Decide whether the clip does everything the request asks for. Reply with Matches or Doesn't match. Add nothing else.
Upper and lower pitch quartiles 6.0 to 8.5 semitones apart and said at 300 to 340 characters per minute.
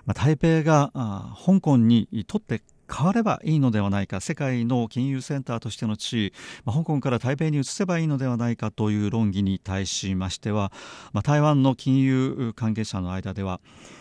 Doesn't match